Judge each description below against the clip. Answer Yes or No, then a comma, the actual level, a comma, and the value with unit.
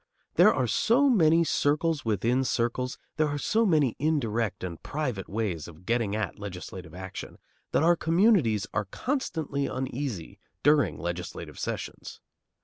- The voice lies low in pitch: Yes, low, 125 Hz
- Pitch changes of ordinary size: No, wide, 7.7 semitones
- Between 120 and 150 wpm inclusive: Yes, average, 140 wpm